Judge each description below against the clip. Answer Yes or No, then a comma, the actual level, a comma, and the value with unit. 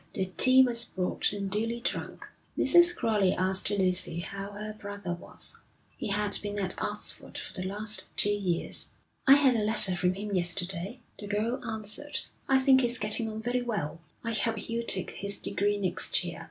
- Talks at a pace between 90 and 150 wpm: No, average, 180 wpm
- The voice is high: Yes, high, 205 Hz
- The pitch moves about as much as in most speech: Yes, average, 3.3 semitones